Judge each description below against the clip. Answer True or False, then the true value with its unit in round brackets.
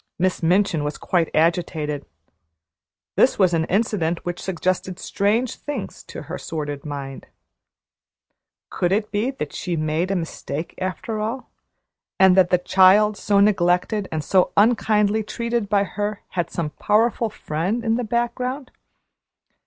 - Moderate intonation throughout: True (4.2 semitones)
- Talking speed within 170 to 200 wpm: False (145 wpm)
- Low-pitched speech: False (190 Hz)